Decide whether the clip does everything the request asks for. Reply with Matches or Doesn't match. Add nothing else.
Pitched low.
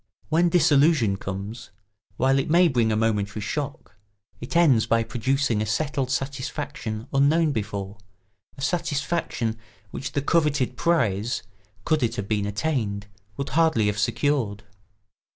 Matches